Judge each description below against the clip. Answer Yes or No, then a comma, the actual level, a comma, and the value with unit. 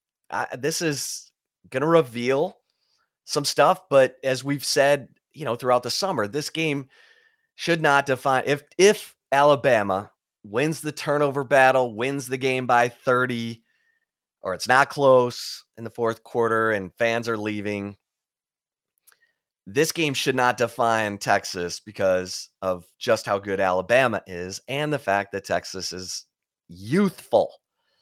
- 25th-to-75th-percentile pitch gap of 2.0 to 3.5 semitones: No, average, 4.8 semitones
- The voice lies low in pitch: Yes, low, 130 Hz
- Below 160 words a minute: Yes, average, 140 wpm